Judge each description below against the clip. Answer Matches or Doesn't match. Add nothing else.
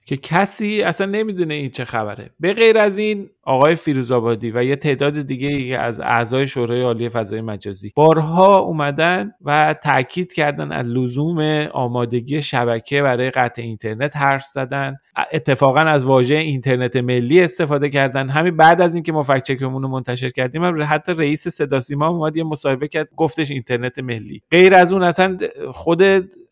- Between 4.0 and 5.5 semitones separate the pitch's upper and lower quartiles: Matches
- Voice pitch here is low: Doesn't match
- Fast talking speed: Matches